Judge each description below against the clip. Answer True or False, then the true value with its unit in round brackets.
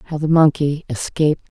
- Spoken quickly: False (160 wpm)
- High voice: False (150 Hz)